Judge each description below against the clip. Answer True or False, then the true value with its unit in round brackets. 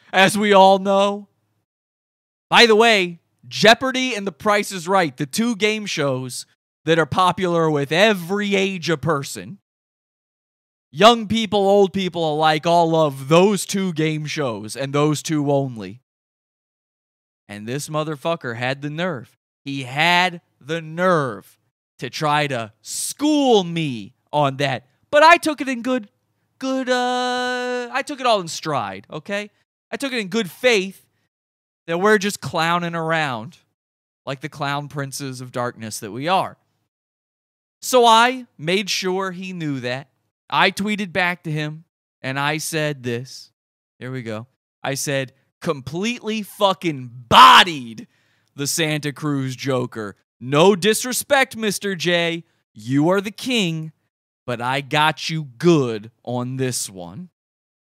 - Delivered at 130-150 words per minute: True (140 wpm)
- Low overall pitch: False (160 Hz)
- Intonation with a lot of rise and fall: True (6.9 semitones)